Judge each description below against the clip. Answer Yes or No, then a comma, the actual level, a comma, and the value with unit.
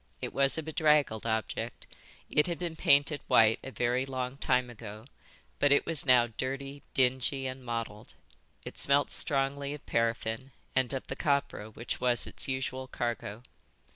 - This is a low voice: Yes, low, 130 Hz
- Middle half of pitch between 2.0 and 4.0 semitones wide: Yes, average, 2.9 semitones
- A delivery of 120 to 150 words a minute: No, average, 160 wpm